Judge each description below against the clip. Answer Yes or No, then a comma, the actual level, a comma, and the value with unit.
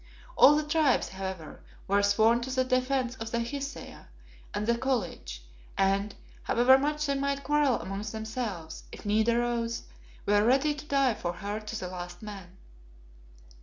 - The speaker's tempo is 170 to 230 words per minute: No, average, 160 wpm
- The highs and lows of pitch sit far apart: No, average, 4.9 semitones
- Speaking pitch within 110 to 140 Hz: No, high, 235 Hz